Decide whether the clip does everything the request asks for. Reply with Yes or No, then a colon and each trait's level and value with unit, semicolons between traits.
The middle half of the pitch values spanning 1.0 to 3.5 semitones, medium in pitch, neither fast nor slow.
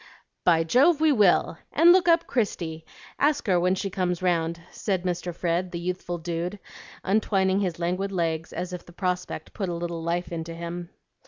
Yes: narrow, 2.4 semitones; medium, 180 Hz; average, 180 wpm